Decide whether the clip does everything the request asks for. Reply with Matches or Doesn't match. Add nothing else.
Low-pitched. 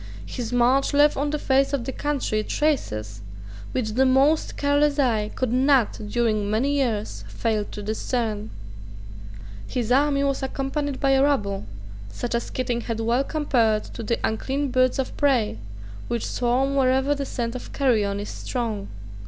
Doesn't match